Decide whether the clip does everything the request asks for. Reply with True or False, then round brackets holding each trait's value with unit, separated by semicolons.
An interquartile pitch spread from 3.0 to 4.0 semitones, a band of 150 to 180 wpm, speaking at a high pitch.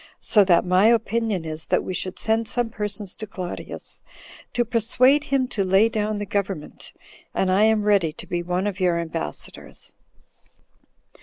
True (3.5 semitones; 165 wpm; 205 Hz)